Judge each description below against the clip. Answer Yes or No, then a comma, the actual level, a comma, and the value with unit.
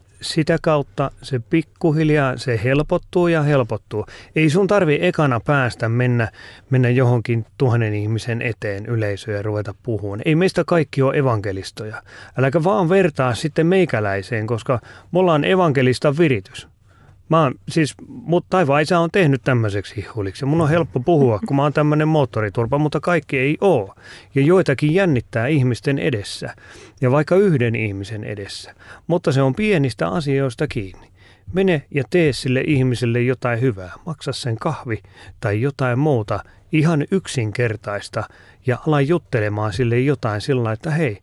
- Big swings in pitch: Yes, wide, 6.0 semitones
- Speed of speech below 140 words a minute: No, average, 145 wpm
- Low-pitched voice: Yes, low, 130 Hz